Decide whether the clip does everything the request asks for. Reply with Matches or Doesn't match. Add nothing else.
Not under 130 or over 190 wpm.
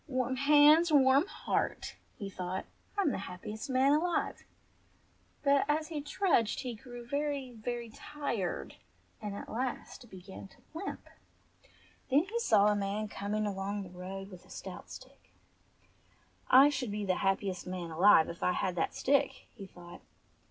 Matches